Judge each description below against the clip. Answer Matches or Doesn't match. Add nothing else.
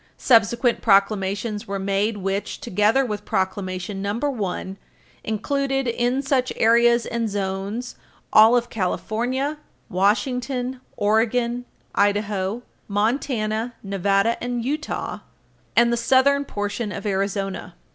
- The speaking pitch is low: Doesn't match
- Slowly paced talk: Matches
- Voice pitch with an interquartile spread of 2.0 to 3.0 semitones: Doesn't match